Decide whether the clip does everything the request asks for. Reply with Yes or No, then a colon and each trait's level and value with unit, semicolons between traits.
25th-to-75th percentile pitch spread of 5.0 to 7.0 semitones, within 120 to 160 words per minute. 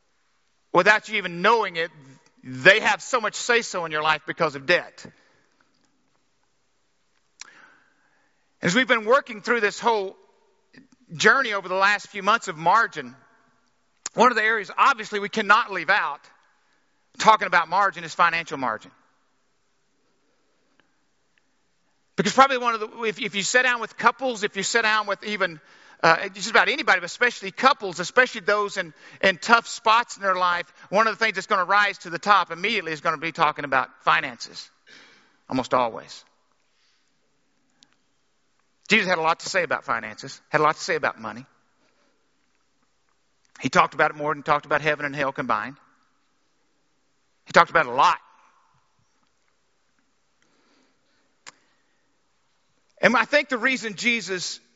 Yes: average, 5.3 semitones; average, 155 wpm